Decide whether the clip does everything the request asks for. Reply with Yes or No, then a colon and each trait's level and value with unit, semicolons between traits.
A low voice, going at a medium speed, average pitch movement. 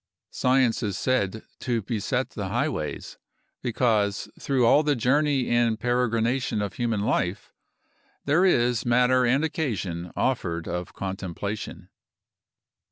No: low, 120 Hz; slow, 115 wpm; average, 4.1 semitones